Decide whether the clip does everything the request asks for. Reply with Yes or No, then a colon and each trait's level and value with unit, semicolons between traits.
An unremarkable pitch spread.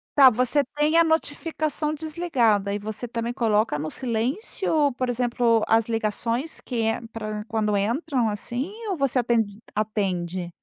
Yes: average, 5.0 semitones